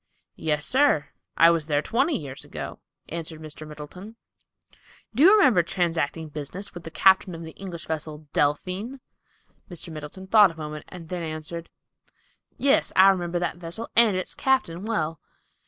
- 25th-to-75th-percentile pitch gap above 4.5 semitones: No, average, 3.9 semitones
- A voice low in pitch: No, medium, 170 Hz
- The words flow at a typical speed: Yes, average, 155 wpm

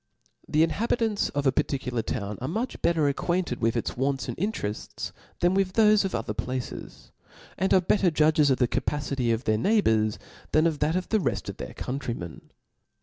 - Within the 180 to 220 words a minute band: Yes, average, 190 wpm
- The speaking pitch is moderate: Yes, medium, 150 Hz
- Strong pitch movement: Yes, wide, 7.1 semitones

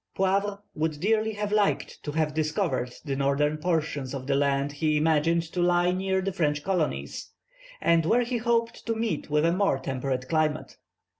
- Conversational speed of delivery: Yes, average, 175 wpm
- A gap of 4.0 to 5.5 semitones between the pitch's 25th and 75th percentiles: Yes, average, 4.7 semitones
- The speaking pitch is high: No, medium, 160 Hz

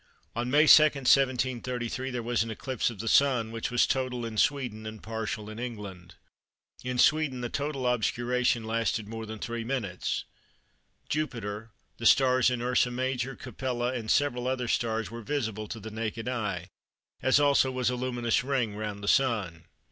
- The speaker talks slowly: No, average, 170 wpm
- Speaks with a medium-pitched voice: No, low, 120 Hz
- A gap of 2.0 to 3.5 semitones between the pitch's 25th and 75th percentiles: Yes, narrow, 2.6 semitones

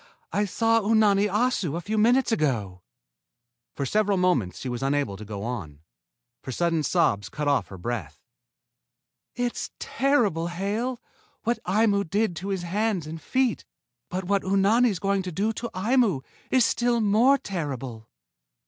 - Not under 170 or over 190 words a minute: No, average, 150 wpm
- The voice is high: Yes, high, 195 Hz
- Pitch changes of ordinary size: No, wide, 7.6 semitones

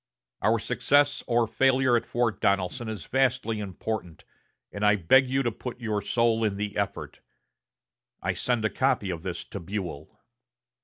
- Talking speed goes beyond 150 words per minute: Yes, average, 160 wpm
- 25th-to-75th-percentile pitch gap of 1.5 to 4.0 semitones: Yes, average, 3.6 semitones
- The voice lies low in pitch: Yes, low, 110 Hz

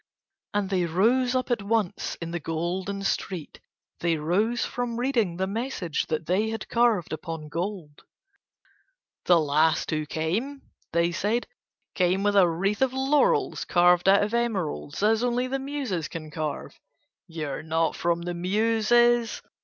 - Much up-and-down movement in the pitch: Yes, wide, 5.7 semitones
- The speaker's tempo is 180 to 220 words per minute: No, average, 155 wpm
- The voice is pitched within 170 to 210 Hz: Yes, high, 190 Hz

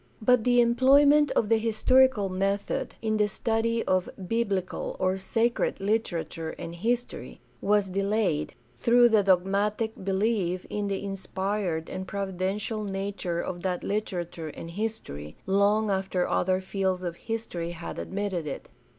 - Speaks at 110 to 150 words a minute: Yes, slow, 135 wpm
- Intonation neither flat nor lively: Yes, average, 3.1 semitones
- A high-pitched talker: Yes, high, 200 Hz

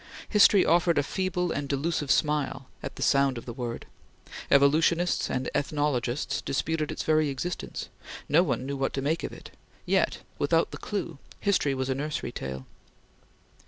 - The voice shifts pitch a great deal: No, average, 3.4 semitones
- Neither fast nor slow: Yes, average, 160 wpm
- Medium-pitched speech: Yes, medium, 145 Hz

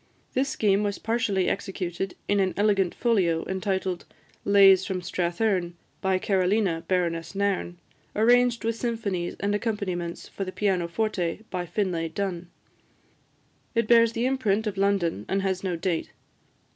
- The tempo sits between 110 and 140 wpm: Yes, slow, 135 wpm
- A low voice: No, high, 195 Hz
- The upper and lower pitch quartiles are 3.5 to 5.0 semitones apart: No, average, 2.9 semitones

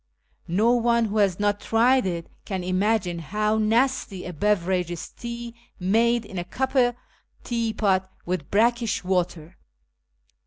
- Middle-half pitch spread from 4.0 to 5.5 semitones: Yes, average, 4.3 semitones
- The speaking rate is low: Yes, slow, 130 wpm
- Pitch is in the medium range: No, high, 210 Hz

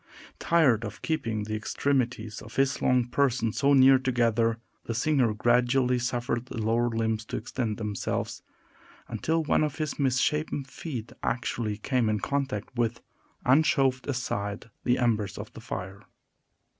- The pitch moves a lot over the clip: No, average, 3.3 semitones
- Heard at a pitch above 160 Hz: No, low, 120 Hz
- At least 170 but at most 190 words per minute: No, average, 145 wpm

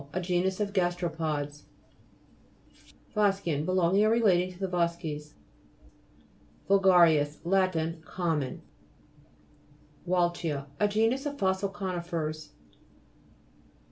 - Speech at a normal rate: No, slow, 80 wpm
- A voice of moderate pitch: Yes, medium, 180 Hz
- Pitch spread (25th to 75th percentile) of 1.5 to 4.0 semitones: Yes, average, 2.9 semitones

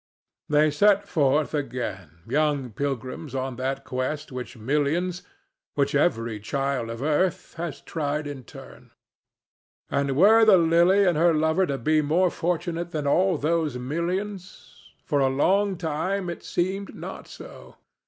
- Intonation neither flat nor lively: Yes, average, 4.3 semitones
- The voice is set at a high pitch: No, medium, 155 Hz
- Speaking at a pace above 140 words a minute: No, slow, 135 wpm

